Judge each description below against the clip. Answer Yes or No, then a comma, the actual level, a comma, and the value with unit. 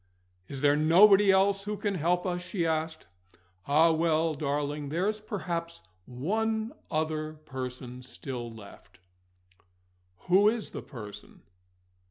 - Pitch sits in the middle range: Yes, medium, 160 Hz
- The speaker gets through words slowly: Yes, slow, 120 wpm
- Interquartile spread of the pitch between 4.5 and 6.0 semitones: Yes, average, 5.2 semitones